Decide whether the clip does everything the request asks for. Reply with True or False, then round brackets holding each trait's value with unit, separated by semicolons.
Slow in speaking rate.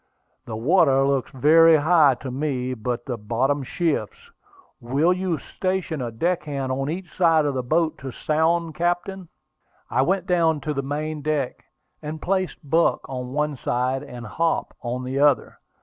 False (165 wpm)